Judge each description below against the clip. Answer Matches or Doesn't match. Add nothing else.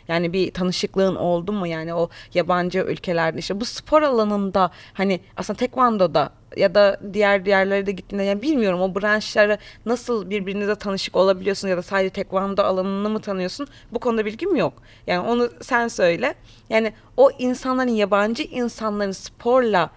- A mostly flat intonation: Doesn't match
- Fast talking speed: Matches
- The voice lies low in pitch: Doesn't match